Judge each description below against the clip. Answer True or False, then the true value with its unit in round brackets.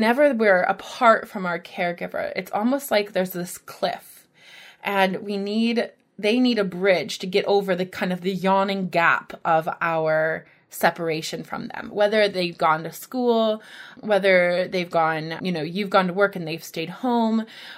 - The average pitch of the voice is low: False (195 Hz)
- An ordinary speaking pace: True (170 wpm)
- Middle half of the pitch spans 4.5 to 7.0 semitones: False (3.6 semitones)